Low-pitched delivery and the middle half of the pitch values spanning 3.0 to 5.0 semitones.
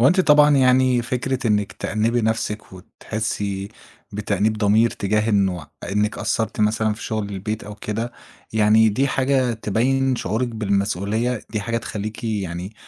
No: low, 110 Hz; narrow, 2.6 semitones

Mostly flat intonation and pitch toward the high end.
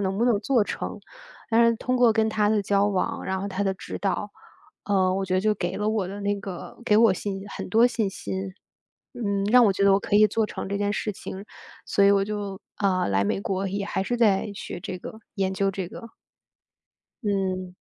Yes: narrow, 1.8 semitones; high, 200 Hz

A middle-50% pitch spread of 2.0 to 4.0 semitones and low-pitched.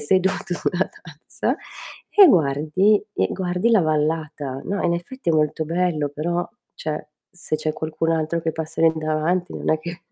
No: narrow, 2.6 semitones; medium, 165 Hz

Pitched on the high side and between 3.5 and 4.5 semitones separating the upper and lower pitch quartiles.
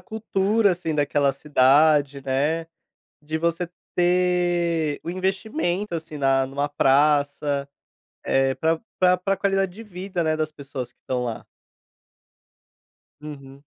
No: medium, 155 Hz; average, 4.2 semitones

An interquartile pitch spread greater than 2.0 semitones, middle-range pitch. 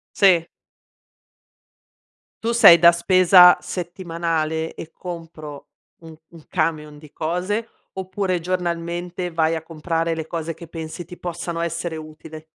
No: narrow, 1.7 semitones; medium, 170 Hz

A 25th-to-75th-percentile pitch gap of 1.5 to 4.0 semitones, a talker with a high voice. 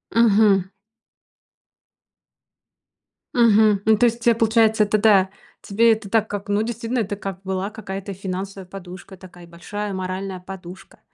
Yes: narrow, 2.6 semitones; high, 200 Hz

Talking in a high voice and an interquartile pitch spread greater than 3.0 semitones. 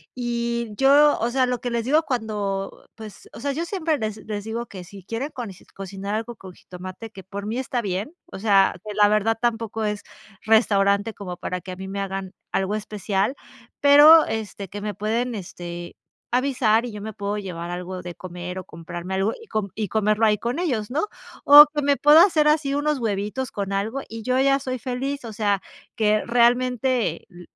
Yes: high, 220 Hz; average, 4.2 semitones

